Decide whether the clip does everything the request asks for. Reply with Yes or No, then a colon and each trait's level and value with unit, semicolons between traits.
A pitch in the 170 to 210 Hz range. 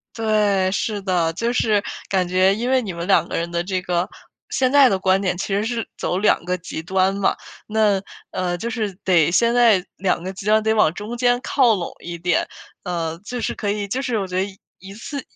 Yes: high, 195 Hz